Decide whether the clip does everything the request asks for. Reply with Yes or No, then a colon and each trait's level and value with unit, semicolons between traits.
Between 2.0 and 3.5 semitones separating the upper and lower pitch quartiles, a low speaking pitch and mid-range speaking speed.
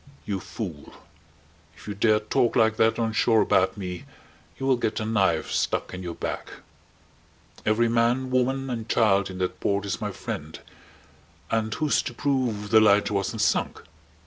Yes: average, 2.9 semitones; low, 110 Hz; average, 170 wpm